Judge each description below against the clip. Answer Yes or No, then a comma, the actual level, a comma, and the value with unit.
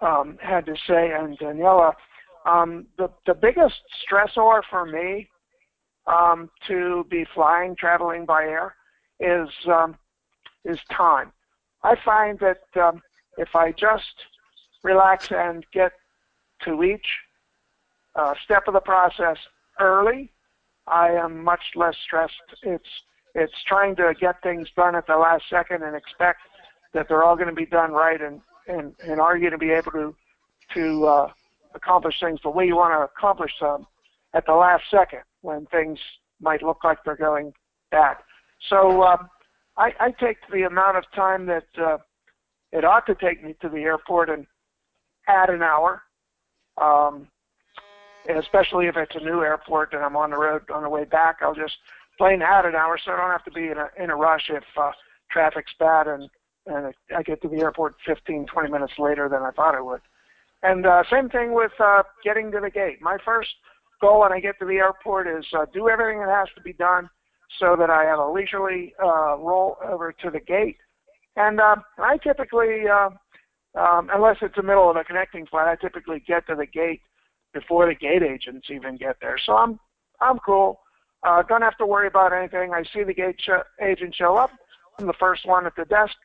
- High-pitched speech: No, medium, 175 Hz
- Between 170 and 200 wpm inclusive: Yes, average, 185 wpm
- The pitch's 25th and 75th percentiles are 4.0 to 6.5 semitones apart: No, average, 3.5 semitones